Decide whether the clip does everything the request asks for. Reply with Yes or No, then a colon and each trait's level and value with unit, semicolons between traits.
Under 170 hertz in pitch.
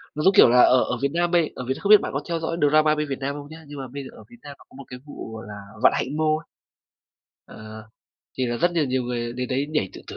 Yes: medium, 140 Hz